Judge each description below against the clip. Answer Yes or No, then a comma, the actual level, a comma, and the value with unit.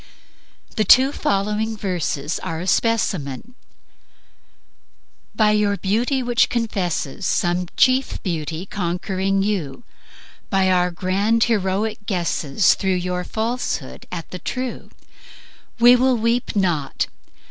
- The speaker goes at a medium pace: No, slow, 110 wpm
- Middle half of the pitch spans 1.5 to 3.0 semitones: No, average, 4.2 semitones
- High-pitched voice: Yes, high, 195 Hz